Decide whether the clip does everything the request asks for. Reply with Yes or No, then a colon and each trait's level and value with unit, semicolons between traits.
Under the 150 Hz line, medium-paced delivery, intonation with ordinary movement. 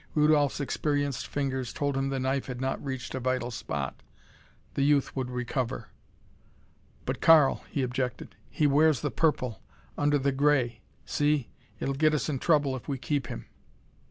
No: low, 135 Hz; average, 160 wpm; narrow, 2.2 semitones